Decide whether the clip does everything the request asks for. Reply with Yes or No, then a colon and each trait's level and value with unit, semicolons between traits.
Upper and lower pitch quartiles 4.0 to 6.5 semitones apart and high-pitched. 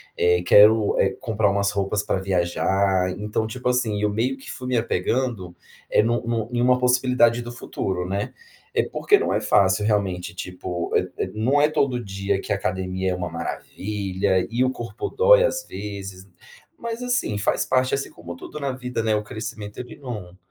No: average, 4.5 semitones; low, 105 Hz